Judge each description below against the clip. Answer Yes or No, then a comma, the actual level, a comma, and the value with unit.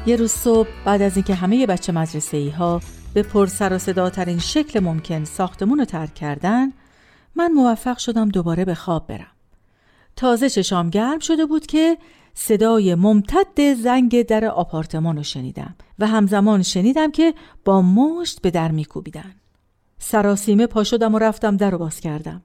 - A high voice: Yes, high, 200 Hz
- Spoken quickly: Yes, fast, 160 wpm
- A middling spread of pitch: No, wide, 6.1 semitones